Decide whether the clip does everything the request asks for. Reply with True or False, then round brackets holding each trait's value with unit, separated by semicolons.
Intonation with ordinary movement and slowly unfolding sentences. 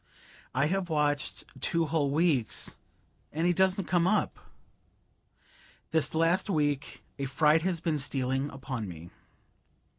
True (3.6 semitones; 125 wpm)